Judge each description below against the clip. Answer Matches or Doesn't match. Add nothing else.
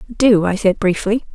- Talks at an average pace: Matches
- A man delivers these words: Doesn't match